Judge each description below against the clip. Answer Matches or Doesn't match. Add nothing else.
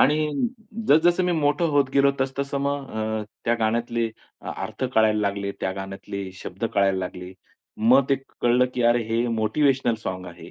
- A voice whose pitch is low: Matches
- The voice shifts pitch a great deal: Matches